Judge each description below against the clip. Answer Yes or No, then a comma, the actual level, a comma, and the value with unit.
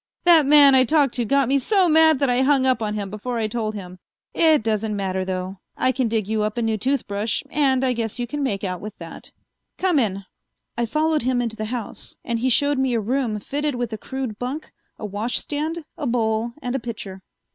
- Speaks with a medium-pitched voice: No, high, 240 Hz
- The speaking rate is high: Yes, fast, 225 wpm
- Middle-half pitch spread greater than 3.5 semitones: Yes, average, 4.4 semitones